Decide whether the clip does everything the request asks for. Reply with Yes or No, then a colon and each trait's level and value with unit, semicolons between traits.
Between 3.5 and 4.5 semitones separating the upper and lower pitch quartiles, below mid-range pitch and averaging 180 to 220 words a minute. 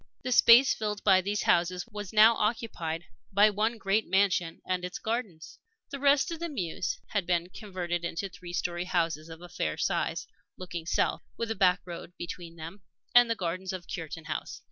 No: average, 3.8 semitones; medium, 185 Hz; average, 190 wpm